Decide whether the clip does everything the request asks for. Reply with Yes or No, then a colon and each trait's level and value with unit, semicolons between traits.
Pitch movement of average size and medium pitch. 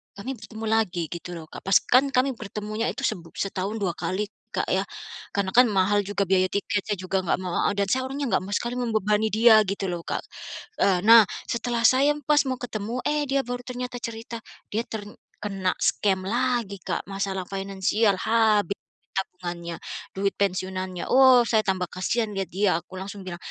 No: average, 3.7 semitones; high, 205 Hz